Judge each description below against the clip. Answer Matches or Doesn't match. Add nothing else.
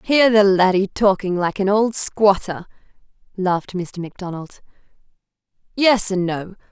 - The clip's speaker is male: Doesn't match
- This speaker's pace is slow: Matches